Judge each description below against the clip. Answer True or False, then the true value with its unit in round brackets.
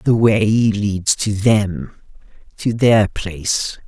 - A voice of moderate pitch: False (105 Hz)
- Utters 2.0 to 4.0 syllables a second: True (2.8 syllables/s)